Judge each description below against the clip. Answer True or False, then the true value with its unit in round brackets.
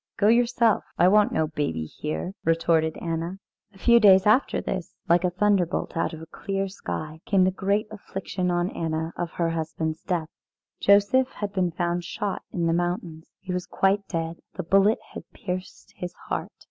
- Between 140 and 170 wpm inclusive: False (180 wpm)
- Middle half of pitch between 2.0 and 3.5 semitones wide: True (3.2 semitones)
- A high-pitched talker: False (180 Hz)